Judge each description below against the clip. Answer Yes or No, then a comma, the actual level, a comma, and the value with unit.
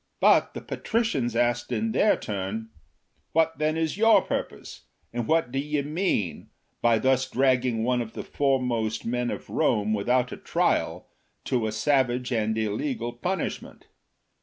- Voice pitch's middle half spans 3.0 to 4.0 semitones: No, average, 4.7 semitones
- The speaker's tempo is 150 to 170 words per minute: Yes, average, 155 wpm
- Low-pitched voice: Yes, low, 125 Hz